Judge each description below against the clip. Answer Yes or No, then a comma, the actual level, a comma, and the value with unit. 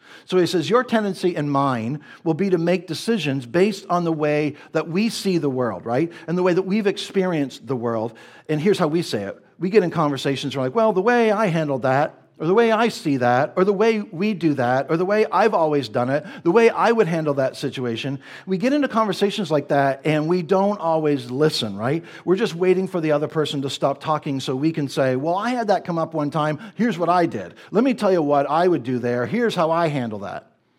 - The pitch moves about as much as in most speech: No, wide, 5.8 semitones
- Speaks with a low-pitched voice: No, medium, 165 Hz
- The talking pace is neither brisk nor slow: No, fast, 245 wpm